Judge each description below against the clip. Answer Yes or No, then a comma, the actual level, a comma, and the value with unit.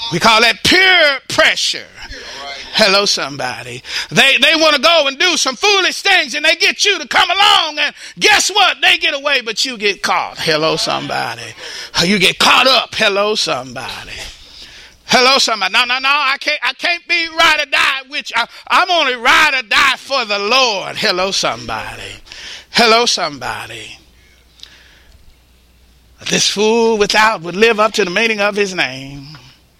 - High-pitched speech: Yes, high, 235 Hz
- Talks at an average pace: Yes, average, 160 wpm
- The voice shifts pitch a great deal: Yes, wide, 8.6 semitones